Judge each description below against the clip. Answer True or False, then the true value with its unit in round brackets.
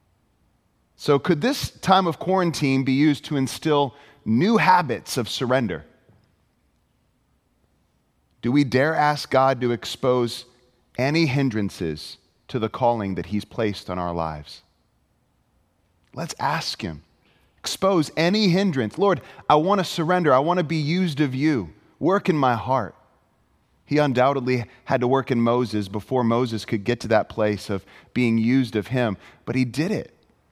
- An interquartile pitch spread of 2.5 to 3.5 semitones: False (5.1 semitones)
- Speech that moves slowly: False (150 wpm)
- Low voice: True (130 Hz)